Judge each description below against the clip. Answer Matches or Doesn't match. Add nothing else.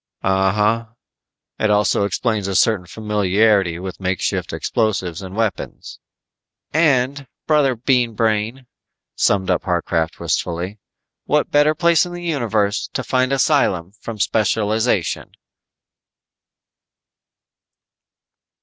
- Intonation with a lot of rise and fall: Doesn't match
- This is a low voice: Matches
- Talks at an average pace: Doesn't match